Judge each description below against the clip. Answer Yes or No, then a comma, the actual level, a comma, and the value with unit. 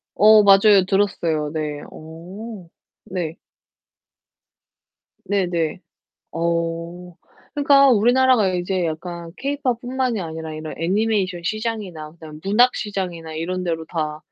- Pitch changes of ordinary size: Yes, average, 4.6 semitones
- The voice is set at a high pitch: No, medium, 180 Hz